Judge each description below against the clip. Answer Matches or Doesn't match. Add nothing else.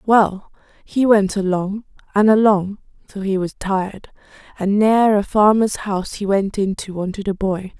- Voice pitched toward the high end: Matches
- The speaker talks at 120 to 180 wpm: Matches